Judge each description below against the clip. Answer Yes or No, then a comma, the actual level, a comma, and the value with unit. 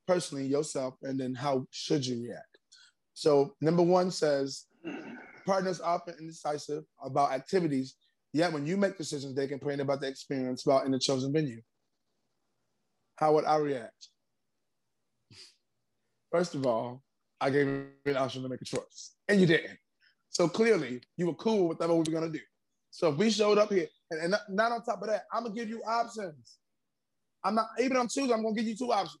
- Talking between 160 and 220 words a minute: Yes, average, 195 wpm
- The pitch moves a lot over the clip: Yes, wide, 7.2 semitones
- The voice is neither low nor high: Yes, medium, 160 Hz